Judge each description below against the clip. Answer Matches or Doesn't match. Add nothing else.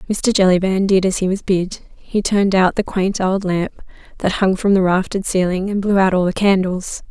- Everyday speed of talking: Doesn't match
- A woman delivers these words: Matches